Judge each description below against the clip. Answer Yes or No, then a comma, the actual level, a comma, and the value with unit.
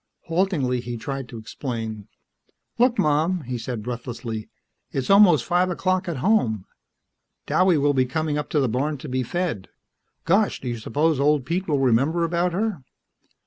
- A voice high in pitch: No, medium, 145 Hz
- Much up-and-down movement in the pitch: Yes, wide, 5.9 semitones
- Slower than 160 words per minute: No, average, 165 wpm